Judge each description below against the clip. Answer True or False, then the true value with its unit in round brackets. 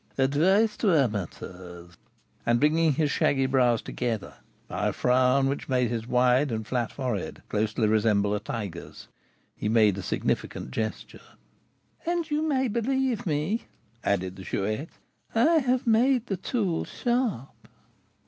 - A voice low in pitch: True (130 Hz)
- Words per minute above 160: False (140 wpm)